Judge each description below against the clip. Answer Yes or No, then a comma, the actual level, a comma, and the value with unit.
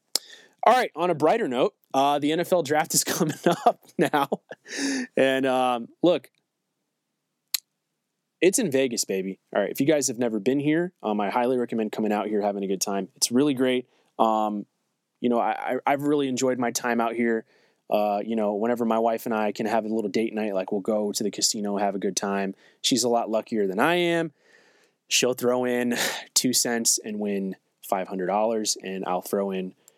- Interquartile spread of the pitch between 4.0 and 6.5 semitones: Yes, average, 4.6 semitones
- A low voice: Yes, low, 120 Hz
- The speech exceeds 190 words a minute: Yes, average, 200 wpm